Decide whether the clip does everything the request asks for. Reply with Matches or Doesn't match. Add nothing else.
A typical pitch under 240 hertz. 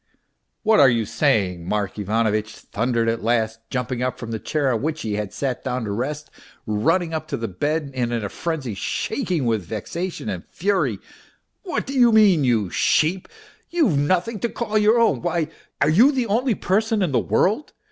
Matches